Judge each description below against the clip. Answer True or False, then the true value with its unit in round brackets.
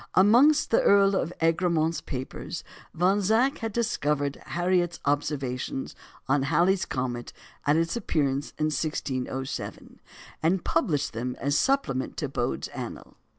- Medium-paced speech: False (130 wpm)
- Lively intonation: True (5.8 semitones)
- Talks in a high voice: False (160 Hz)